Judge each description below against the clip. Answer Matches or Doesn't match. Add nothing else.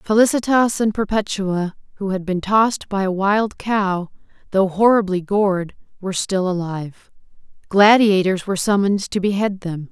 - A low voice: Doesn't match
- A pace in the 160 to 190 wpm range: Doesn't match